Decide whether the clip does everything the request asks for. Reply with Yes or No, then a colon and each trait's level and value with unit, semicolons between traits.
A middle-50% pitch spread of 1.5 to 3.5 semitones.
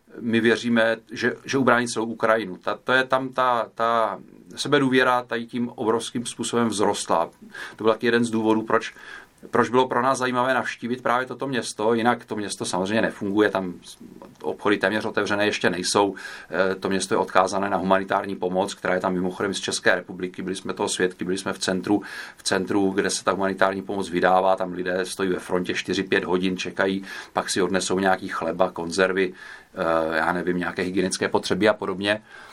No: average, 3.9 semitones